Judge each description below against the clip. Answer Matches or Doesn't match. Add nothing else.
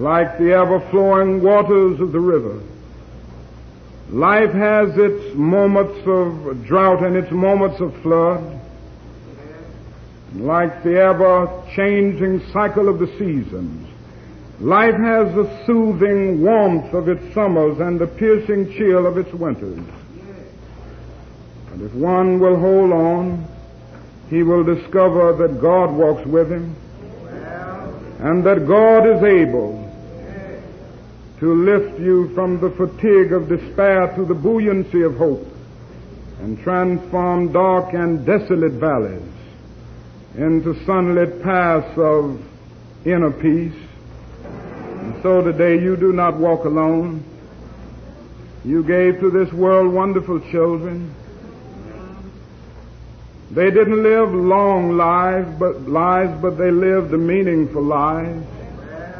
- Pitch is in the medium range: Matches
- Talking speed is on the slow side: Matches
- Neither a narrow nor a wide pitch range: Matches